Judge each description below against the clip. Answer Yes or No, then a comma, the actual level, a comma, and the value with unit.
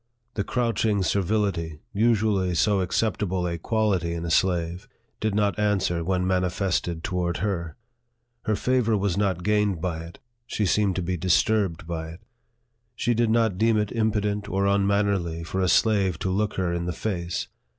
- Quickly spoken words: No, average, 170 wpm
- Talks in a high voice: No, very low, 95 Hz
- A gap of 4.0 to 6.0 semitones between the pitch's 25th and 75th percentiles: No, average, 3.4 semitones